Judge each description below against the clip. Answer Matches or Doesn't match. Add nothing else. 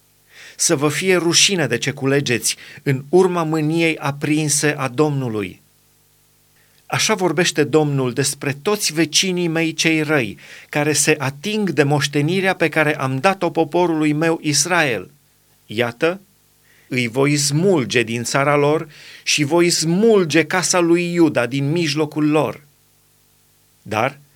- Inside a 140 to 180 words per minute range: Doesn't match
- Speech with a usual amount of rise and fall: Matches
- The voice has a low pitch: Doesn't match